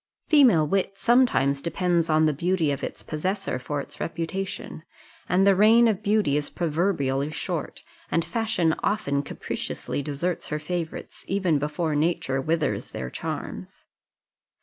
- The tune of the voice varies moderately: Yes, average, 4.7 semitones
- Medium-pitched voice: Yes, medium, 165 Hz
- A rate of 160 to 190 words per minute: No, average, 140 wpm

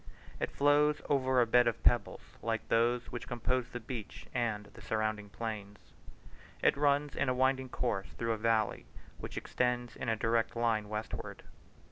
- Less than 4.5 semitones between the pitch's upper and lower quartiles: Yes, narrow, 2.5 semitones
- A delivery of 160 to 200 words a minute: Yes, average, 165 wpm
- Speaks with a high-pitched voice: No, low, 120 Hz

